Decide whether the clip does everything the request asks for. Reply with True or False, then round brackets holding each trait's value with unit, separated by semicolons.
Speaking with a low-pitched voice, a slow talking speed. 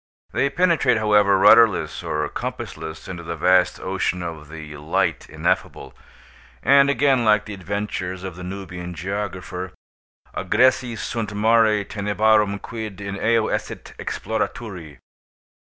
True (100 Hz; 125 wpm)